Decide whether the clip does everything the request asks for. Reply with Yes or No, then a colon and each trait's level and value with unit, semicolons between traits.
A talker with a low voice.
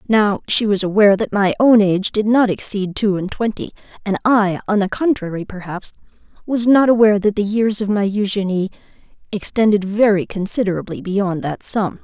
No: high, 205 Hz